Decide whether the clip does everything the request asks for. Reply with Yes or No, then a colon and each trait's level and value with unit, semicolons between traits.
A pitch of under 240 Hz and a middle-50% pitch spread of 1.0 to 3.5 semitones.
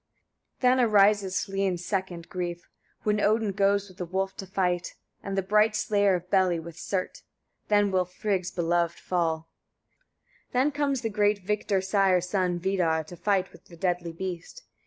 Yes: high, 190 Hz; narrow, 2.6 semitones